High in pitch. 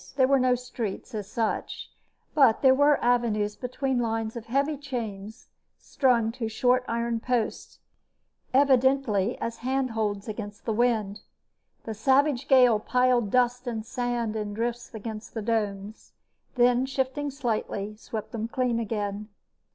Yes: high, 235 Hz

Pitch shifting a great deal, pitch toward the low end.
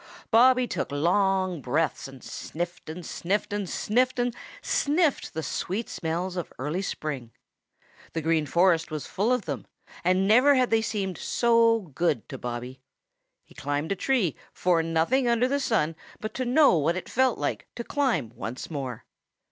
No: wide, 7.0 semitones; medium, 185 Hz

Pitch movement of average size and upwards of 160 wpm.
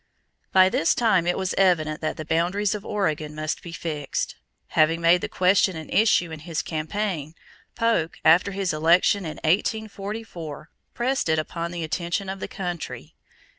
Yes: average, 3.7 semitones; average, 170 wpm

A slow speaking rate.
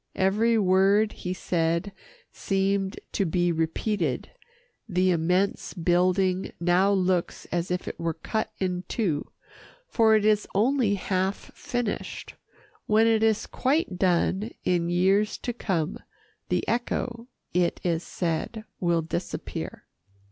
Yes: slow, 125 wpm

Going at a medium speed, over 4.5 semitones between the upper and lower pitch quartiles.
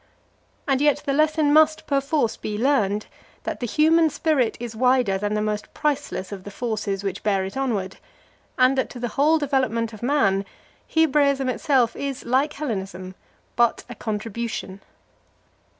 Yes: average, 155 wpm; average, 5.2 semitones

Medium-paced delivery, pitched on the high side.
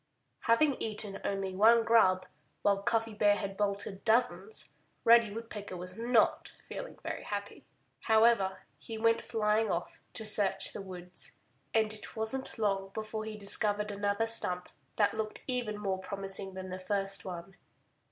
Yes: average, 150 wpm; high, 210 Hz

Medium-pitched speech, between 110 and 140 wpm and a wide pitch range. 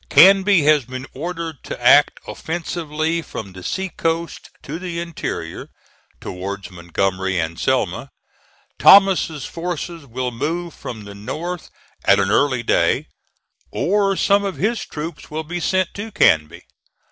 Yes: medium, 160 Hz; slow, 135 wpm; wide, 7.6 semitones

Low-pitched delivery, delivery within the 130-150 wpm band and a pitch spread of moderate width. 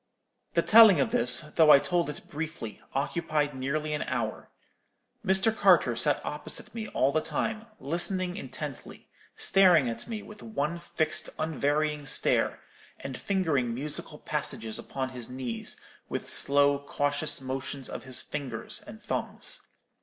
No: medium, 150 Hz; average, 140 wpm; average, 4.4 semitones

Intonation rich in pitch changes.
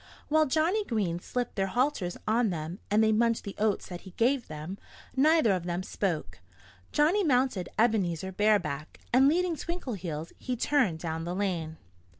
Yes: wide, 6.9 semitones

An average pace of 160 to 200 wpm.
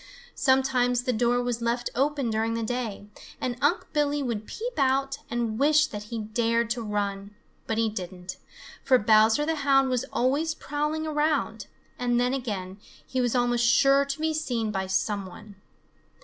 Yes: average, 170 wpm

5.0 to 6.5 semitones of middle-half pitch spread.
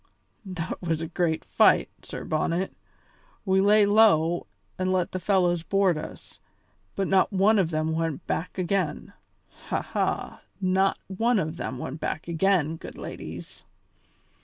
No: average, 3.0 semitones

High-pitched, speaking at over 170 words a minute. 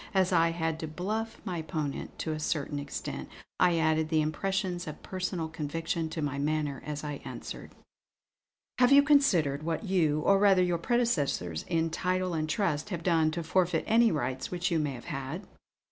No: medium, 165 Hz; average, 180 wpm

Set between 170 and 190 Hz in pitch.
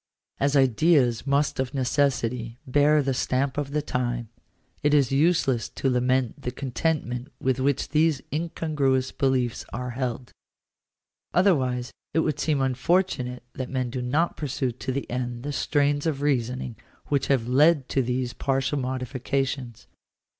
No: low, 130 Hz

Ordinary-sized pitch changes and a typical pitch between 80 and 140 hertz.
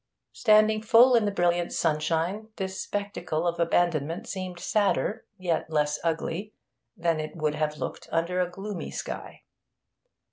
No: average, 3.8 semitones; medium, 175 Hz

